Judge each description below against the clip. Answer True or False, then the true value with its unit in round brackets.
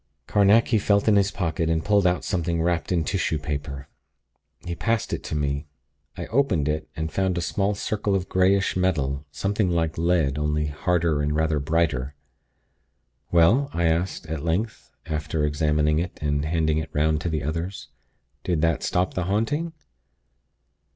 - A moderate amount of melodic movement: True (3.7 semitones)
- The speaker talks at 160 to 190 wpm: True (165 wpm)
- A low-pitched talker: True (80 Hz)